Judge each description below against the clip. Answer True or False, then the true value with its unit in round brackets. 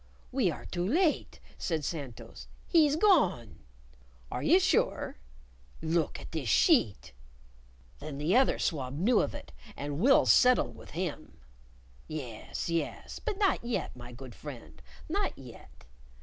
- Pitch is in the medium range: True (170 Hz)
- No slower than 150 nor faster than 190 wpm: False (135 wpm)